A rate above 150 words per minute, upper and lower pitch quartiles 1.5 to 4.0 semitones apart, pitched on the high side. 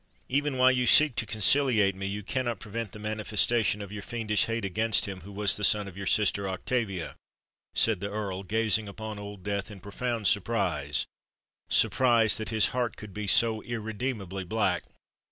No: average, 170 wpm; narrow, 2.6 semitones; low, 105 Hz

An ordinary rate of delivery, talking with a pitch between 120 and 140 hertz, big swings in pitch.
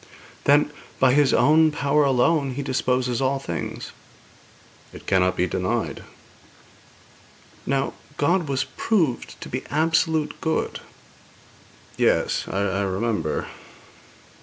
No: slow, 105 wpm; low, 135 Hz; wide, 6.8 semitones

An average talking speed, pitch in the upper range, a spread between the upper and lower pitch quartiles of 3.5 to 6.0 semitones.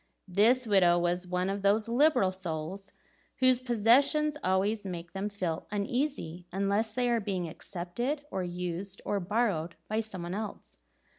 Yes: average, 150 wpm; high, 200 Hz; average, 4.2 semitones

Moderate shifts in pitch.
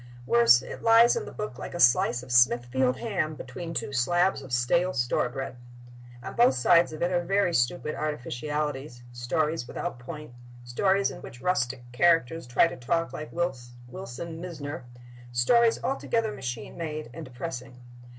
No: wide, 5.9 semitones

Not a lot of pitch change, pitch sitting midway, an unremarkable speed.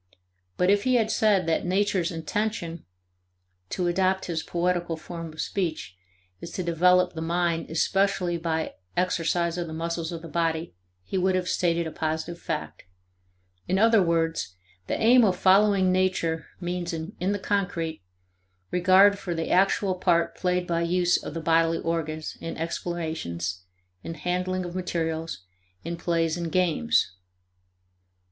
Yes: narrow, 2.1 semitones; medium, 175 Hz; average, 150 wpm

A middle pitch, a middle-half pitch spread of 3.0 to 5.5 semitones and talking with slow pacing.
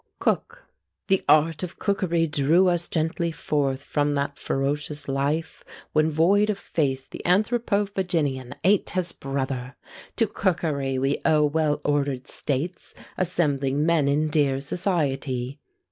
Yes: medium, 150 Hz; average, 3.9 semitones; slow, 130 wpm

